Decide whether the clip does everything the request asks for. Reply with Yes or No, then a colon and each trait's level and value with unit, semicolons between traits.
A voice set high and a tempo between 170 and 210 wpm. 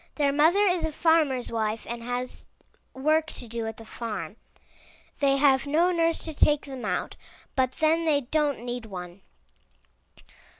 No: very high, 275 Hz; average, 160 wpm